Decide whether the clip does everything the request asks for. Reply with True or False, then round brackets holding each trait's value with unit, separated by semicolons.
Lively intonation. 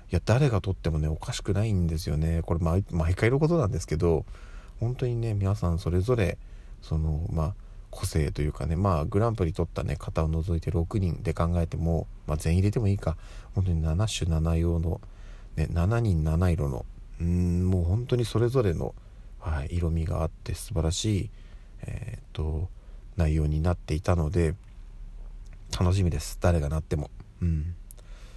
False (3.8 semitones)